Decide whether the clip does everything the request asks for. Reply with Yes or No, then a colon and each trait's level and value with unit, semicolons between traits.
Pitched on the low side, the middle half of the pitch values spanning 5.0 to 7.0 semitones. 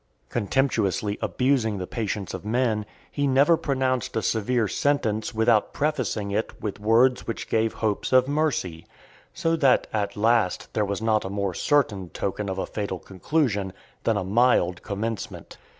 No: low, 110 Hz; average, 4.1 semitones